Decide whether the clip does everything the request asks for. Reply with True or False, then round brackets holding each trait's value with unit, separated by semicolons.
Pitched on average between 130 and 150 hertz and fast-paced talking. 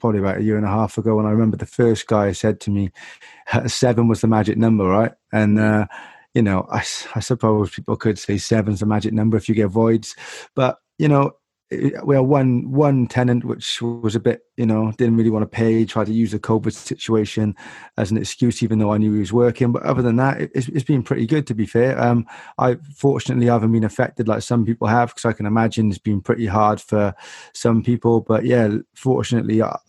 False (115 Hz; 235 wpm)